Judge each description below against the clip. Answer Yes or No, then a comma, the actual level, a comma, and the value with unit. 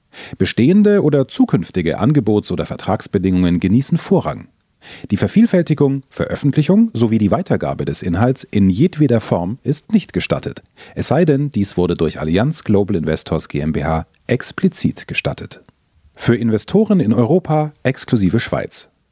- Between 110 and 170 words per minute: Yes, slow, 125 wpm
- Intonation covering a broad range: Yes, wide, 8.8 semitones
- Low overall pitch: Yes, low, 120 Hz